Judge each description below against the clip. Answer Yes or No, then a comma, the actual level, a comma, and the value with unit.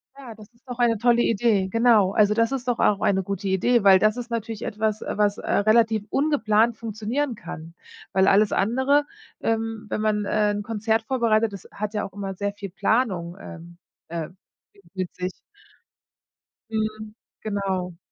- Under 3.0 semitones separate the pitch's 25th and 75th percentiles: Yes, narrow, 2.6 semitones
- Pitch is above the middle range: Yes, high, 215 Hz